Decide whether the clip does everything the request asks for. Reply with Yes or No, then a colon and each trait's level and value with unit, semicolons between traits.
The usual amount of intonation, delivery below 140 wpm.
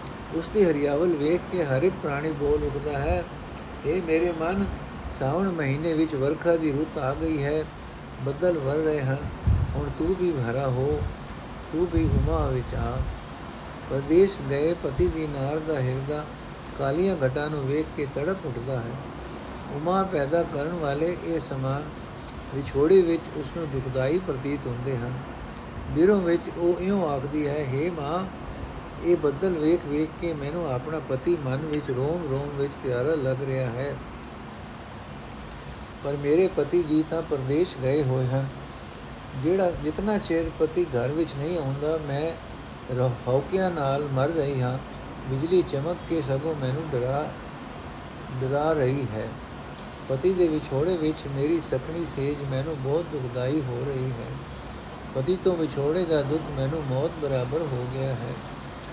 No: average, 3.7 semitones; average, 145 wpm